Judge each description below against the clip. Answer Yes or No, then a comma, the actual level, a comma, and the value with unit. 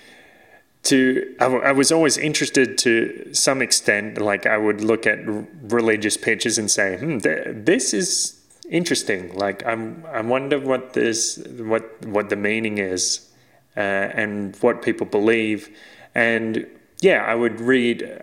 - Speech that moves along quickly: No, average, 150 wpm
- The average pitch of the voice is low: Yes, low, 115 Hz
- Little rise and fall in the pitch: No, average, 3.2 semitones